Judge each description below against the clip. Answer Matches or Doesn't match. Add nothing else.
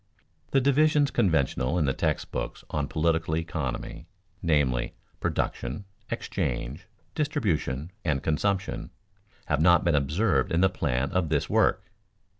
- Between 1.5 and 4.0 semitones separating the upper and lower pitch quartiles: Doesn't match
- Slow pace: Matches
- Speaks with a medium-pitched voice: Doesn't match